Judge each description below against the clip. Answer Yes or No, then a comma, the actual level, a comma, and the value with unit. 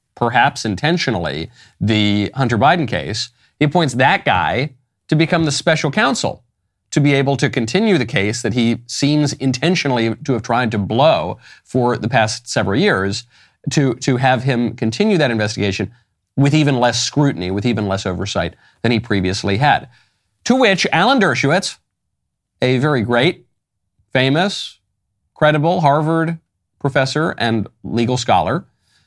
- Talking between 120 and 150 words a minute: Yes, average, 140 wpm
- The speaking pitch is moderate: No, low, 120 Hz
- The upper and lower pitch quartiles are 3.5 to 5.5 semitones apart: Yes, average, 5.2 semitones